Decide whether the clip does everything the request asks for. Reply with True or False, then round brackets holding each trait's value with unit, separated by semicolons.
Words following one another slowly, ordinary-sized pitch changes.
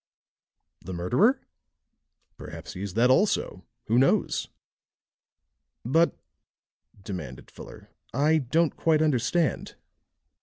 False (90 wpm; 8.0 semitones)